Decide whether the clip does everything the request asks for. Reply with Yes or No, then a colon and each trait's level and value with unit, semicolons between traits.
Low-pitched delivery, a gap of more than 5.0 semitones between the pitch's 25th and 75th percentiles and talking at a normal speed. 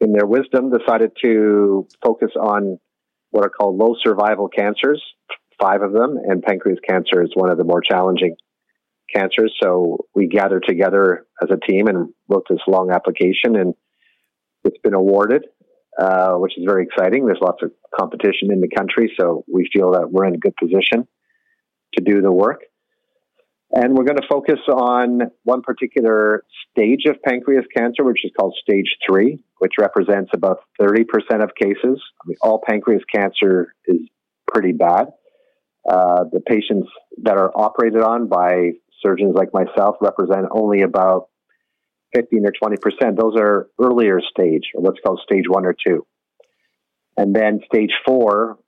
No: low, 110 Hz; average, 4.6 semitones; average, 160 wpm